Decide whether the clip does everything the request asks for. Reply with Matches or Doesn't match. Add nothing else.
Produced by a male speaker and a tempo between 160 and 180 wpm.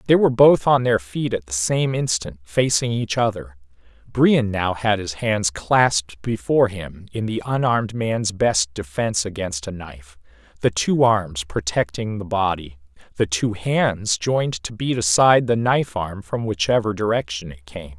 Matches